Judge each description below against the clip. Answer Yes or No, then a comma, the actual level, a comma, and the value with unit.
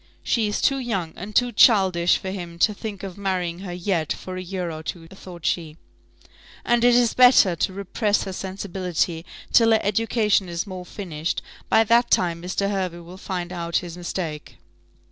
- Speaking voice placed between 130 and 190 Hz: Yes, medium, 185 Hz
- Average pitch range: Yes, average, 3.2 semitones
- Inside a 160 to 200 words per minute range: Yes, average, 185 wpm